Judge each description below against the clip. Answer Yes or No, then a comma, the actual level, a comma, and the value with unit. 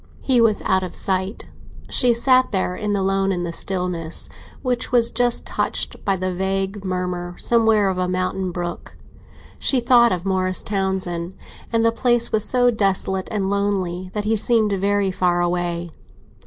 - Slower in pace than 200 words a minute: Yes, average, 160 wpm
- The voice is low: No, high, 195 Hz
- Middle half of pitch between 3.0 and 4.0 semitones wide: Yes, average, 3.3 semitones